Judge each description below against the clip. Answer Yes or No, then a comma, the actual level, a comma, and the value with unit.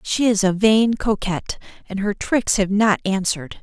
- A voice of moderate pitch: No, high, 205 Hz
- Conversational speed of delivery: Yes, average, 180 wpm